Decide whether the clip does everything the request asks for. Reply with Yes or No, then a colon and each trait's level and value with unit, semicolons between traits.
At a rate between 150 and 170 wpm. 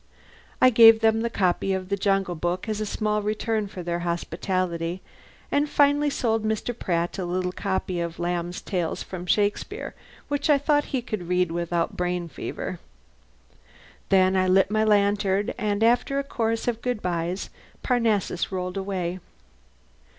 Yes: average, 160 wpm